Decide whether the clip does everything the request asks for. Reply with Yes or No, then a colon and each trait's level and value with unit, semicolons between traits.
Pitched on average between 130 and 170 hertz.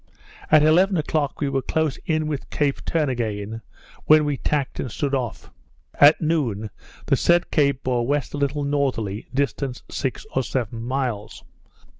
Yes: medium, 140 Hz